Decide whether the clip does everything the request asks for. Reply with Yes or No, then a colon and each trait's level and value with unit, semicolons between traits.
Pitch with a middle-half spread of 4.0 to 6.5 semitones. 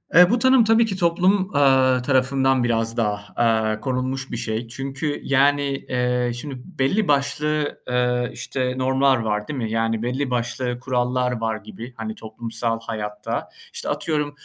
No: average, 3.3 semitones